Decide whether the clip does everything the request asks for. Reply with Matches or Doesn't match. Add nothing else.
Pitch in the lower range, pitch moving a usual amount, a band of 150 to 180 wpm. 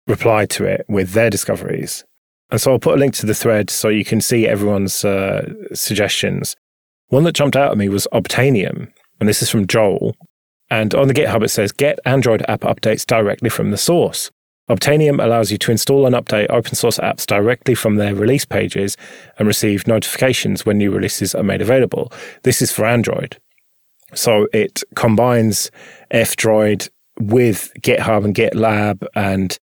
Matches